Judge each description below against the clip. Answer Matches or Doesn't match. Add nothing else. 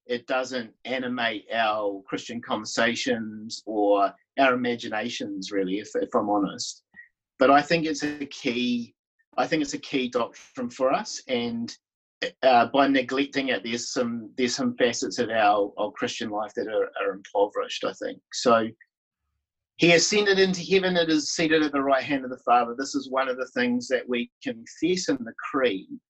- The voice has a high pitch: Doesn't match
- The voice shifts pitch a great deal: Matches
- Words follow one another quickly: Doesn't match